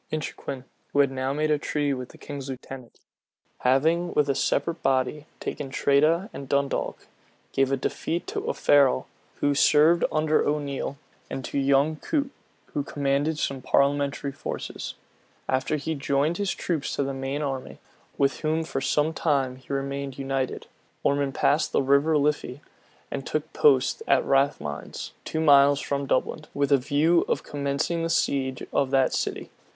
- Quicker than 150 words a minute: Yes, average, 160 wpm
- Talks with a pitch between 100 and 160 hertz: Yes, medium, 140 Hz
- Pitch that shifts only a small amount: Yes, narrow, 2.0 semitones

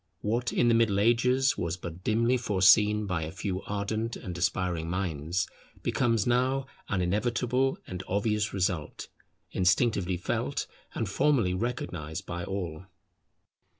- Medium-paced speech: No, slow, 130 wpm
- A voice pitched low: Yes, low, 100 Hz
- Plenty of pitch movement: No, average, 4.4 semitones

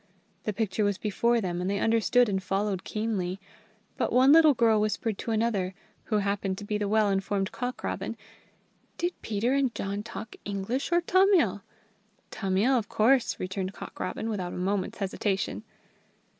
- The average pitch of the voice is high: Yes, high, 210 Hz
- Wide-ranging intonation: No, average, 3.2 semitones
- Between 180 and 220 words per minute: No, average, 165 wpm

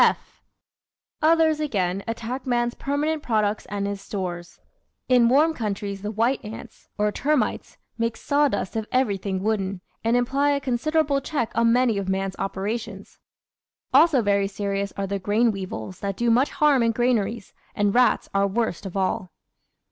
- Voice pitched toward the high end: Yes, high, 225 Hz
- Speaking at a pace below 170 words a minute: Yes, average, 160 wpm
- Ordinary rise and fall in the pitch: Yes, average, 4.3 semitones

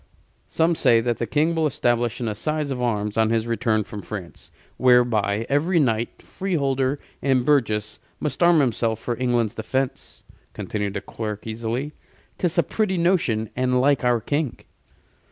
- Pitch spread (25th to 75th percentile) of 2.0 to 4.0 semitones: No, average, 4.6 semitones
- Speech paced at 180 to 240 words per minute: No, average, 155 wpm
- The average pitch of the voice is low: Yes, low, 125 Hz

